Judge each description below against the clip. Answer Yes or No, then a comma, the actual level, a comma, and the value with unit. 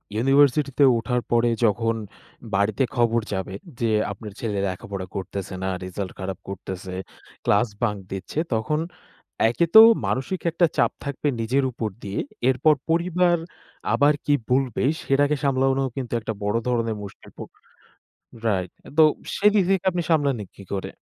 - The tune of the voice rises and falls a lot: Yes, wide, 5.9 semitones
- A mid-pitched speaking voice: No, low, 120 Hz